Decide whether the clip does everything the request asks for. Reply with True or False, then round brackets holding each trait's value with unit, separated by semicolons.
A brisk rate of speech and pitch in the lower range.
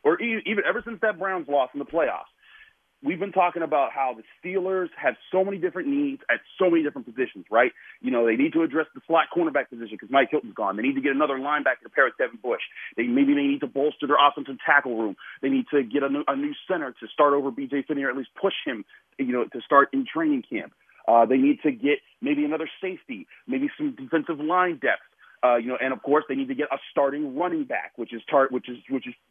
False (250 wpm; 155 Hz)